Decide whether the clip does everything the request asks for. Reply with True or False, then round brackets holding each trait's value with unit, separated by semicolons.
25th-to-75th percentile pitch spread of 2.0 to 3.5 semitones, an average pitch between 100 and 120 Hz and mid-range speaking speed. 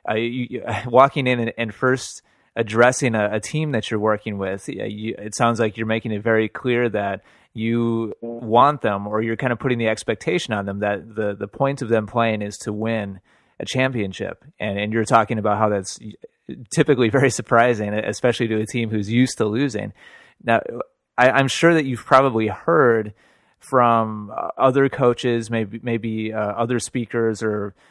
True (2.5 semitones; 115 Hz; 185 wpm)